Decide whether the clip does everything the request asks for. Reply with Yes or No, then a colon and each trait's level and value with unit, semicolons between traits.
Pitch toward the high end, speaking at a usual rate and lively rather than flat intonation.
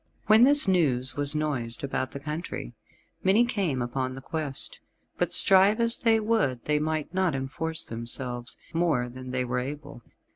No: medium, 150 Hz; average, 160 wpm; wide, 6.4 semitones